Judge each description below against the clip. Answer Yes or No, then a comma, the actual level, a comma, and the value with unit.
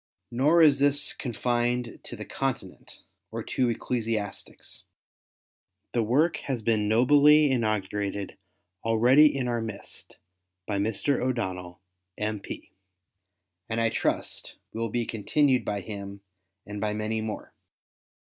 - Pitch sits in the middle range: No, low, 115 Hz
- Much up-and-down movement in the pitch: No, average, 3.5 semitones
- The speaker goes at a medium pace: No, slow, 120 wpm